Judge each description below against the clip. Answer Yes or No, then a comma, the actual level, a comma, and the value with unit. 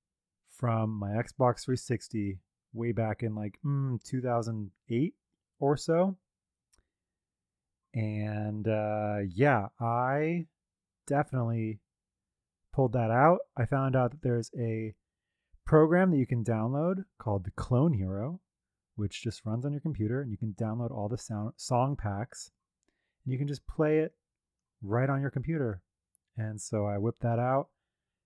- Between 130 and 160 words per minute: Yes, average, 140 wpm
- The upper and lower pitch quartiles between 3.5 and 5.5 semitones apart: Yes, average, 4.4 semitones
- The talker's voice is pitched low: Yes, low, 120 Hz